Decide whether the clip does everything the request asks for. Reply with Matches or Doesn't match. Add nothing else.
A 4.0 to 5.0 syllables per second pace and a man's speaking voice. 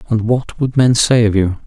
Matches